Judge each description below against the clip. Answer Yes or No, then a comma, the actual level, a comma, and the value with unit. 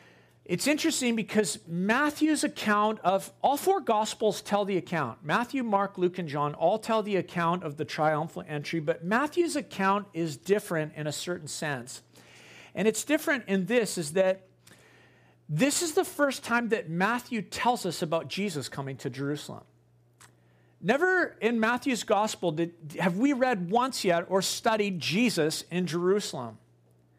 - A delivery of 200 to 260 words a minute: No, average, 155 wpm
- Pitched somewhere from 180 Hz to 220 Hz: Yes, medium, 185 Hz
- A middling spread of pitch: No, wide, 7.0 semitones